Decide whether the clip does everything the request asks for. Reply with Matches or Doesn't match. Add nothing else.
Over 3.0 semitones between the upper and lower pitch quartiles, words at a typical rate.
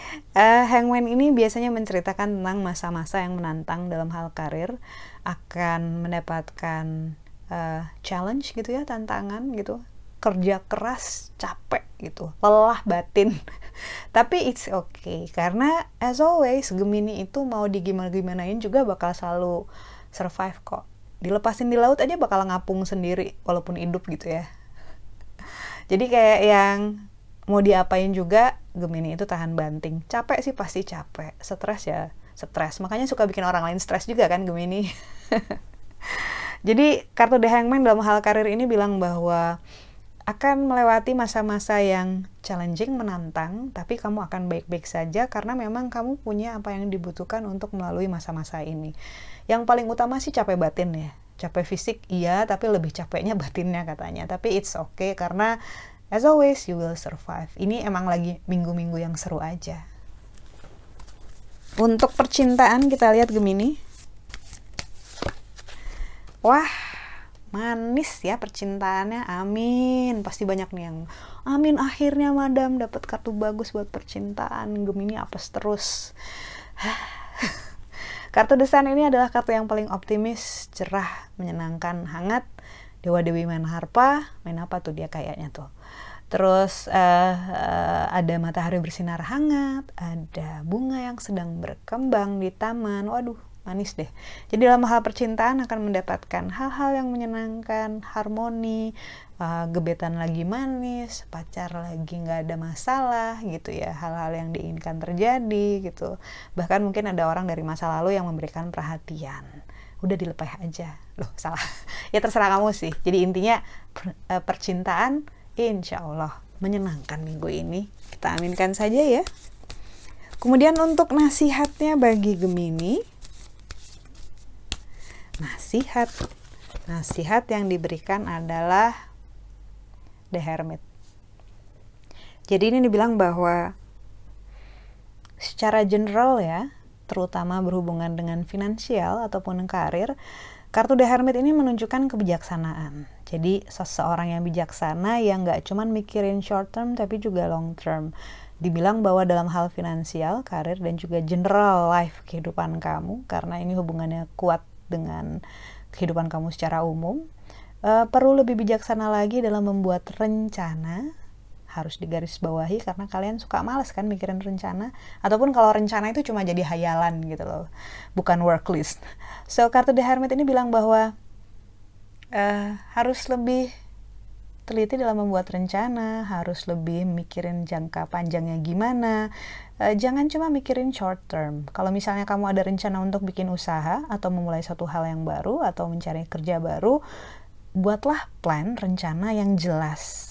Matches